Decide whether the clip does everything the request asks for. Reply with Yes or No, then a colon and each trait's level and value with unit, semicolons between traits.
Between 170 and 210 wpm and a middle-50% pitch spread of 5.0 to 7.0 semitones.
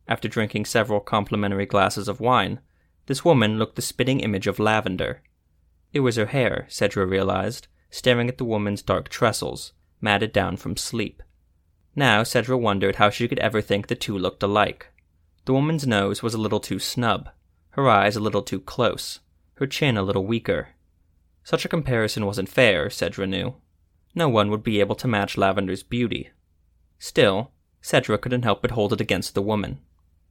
Yes: average, 175 wpm; wide, 5.4 semitones